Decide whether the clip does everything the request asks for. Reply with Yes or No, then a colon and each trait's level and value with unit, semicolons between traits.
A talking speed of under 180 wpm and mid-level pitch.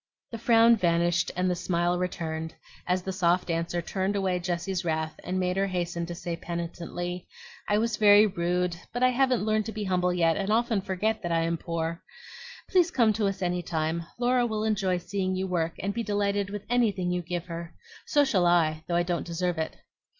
No: fast, 205 wpm; medium, 180 Hz